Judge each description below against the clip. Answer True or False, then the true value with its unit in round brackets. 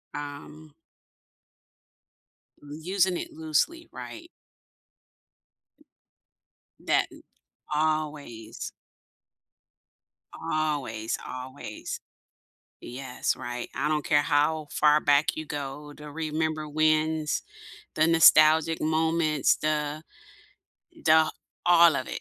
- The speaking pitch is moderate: True (155 Hz)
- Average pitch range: False (1.5 semitones)